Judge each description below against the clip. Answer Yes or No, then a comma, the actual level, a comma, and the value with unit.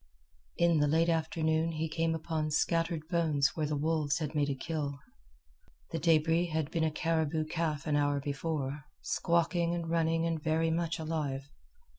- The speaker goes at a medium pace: Yes, average, 165 wpm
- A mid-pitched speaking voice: Yes, medium, 160 Hz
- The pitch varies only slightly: Yes, narrow, 1.7 semitones